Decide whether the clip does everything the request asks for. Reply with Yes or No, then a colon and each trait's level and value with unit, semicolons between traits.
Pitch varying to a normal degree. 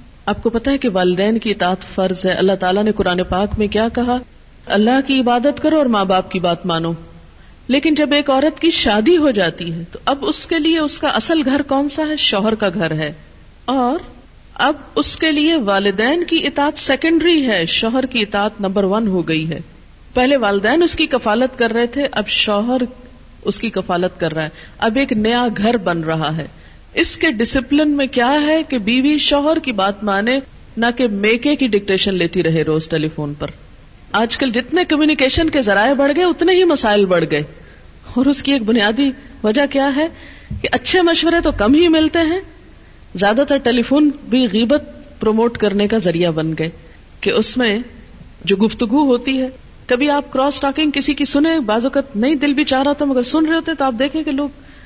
No: wide, 6.2 semitones